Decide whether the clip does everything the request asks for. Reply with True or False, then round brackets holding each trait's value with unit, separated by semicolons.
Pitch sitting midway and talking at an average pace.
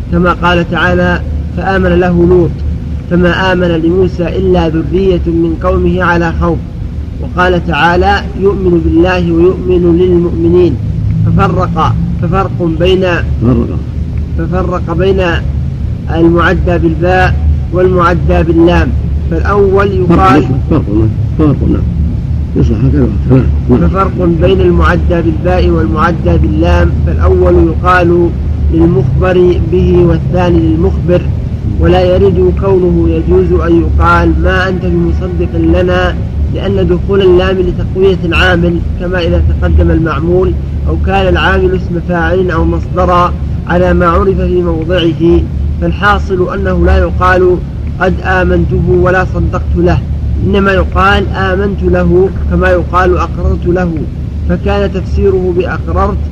False (90 Hz; 100 wpm)